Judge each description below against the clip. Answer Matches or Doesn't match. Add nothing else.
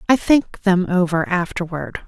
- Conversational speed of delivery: Matches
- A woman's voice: Matches